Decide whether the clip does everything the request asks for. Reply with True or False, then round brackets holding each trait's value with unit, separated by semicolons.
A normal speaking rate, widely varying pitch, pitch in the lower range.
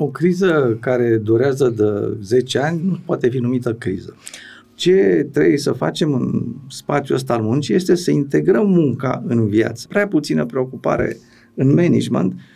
True (155 wpm; 6.6 semitones; 130 Hz)